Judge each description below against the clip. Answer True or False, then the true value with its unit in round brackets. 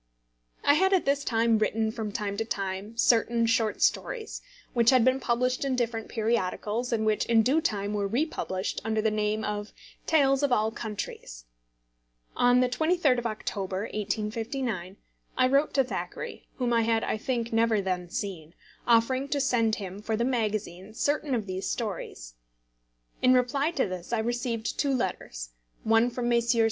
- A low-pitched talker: False (230 Hz)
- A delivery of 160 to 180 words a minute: True (170 wpm)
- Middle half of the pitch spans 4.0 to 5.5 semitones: False (3.2 semitones)